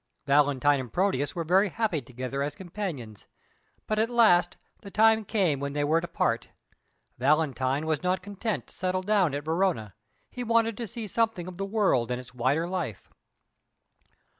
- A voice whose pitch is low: No, medium, 175 Hz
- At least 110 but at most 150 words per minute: No, average, 170 wpm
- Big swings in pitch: Yes, wide, 6.4 semitones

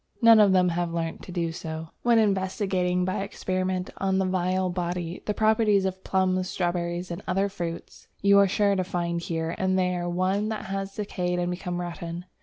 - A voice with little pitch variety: Yes, narrow, 1.8 semitones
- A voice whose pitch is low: No, medium, 185 Hz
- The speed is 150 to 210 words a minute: Yes, average, 190 wpm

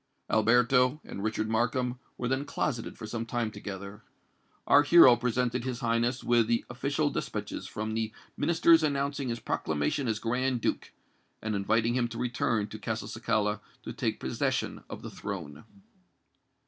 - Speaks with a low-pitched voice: Yes, low, 120 Hz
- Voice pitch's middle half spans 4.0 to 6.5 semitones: No, average, 2.7 semitones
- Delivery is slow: No, average, 150 wpm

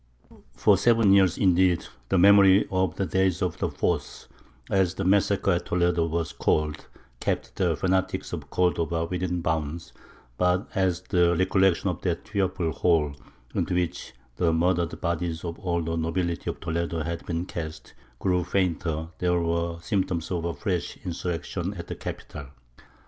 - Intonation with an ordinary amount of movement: No, narrow, 2.0 semitones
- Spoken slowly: No, average, 155 wpm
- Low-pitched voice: Yes, very low, 85 Hz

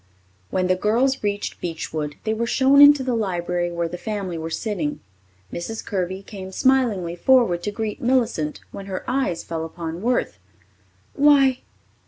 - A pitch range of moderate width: No, wide, 6.0 semitones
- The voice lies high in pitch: Yes, high, 200 Hz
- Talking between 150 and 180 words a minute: Yes, average, 155 wpm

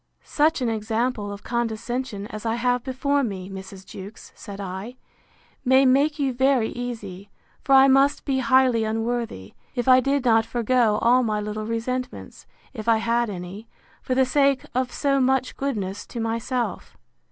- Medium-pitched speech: No, high, 240 Hz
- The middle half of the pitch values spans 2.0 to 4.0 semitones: Yes, average, 3.4 semitones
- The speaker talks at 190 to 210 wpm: No, average, 165 wpm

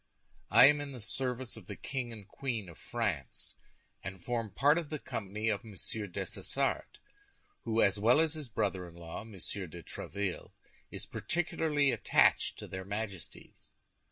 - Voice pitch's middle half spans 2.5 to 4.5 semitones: No, average, 5.2 semitones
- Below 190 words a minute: Yes, average, 160 wpm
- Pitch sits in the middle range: No, low, 110 Hz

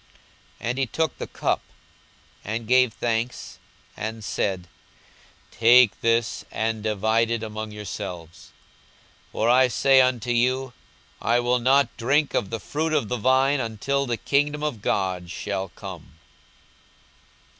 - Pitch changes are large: No, average, 3.2 semitones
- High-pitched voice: No, low, 115 Hz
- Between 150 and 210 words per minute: No, average, 140 wpm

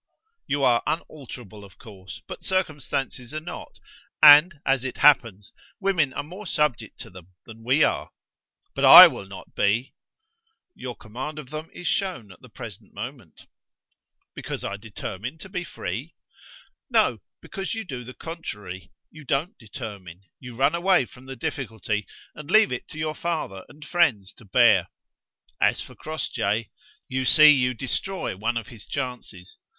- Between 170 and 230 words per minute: No, average, 160 wpm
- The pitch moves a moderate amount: No, wide, 6.1 semitones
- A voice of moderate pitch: No, low, 130 Hz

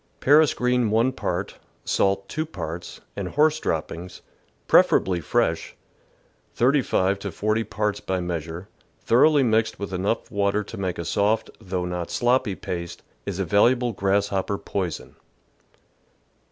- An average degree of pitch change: Yes, average, 4.4 semitones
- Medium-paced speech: No, slow, 130 wpm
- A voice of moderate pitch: No, low, 100 Hz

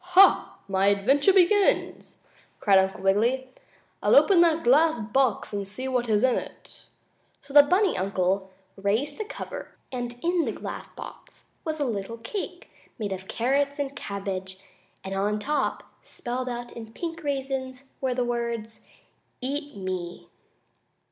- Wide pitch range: Yes, wide, 6.1 semitones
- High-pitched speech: Yes, high, 245 Hz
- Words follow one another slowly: No, average, 150 wpm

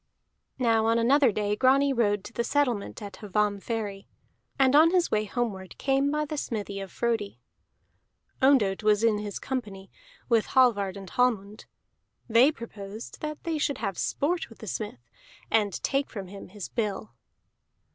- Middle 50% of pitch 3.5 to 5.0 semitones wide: Yes, average, 4.5 semitones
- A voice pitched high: Yes, high, 225 Hz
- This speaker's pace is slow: No, average, 155 wpm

